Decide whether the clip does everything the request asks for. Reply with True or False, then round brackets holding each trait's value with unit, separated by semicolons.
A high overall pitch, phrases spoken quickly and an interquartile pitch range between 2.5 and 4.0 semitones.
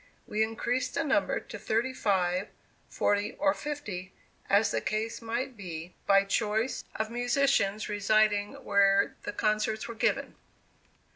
False (215 Hz; 135 wpm; 3.3 semitones)